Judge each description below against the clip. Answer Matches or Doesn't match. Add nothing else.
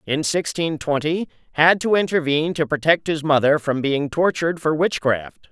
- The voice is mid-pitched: Matches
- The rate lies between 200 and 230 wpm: Doesn't match